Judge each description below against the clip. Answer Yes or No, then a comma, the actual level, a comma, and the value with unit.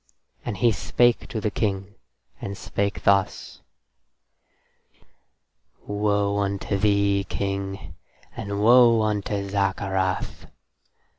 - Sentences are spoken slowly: Yes, slow, 90 wpm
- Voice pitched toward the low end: Yes, low, 100 Hz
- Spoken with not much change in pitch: Yes, narrow, 1.3 semitones